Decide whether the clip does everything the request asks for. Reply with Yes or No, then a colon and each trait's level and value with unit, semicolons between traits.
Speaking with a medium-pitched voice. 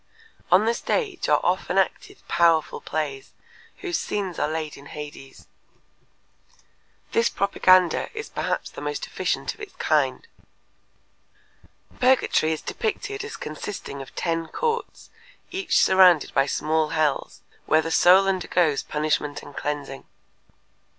Yes: medium, 170 Hz